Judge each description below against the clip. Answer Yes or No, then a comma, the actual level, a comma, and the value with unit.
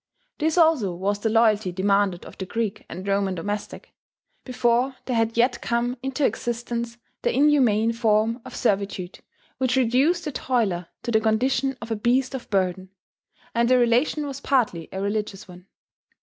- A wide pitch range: No, average, 4.0 semitones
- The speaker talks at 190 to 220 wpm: No, average, 165 wpm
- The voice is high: Yes, high, 230 Hz